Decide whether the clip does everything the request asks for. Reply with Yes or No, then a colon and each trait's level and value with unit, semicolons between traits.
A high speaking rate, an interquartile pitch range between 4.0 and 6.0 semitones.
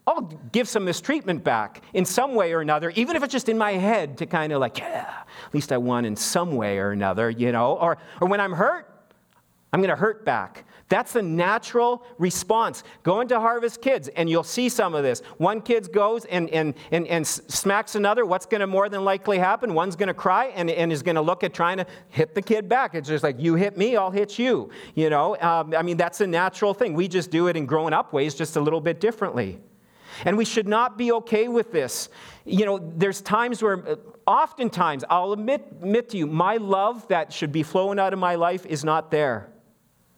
Yes: fast, 225 wpm; average, 5.3 semitones